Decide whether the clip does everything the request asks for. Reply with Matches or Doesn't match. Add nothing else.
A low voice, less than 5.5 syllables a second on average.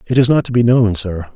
Doesn't match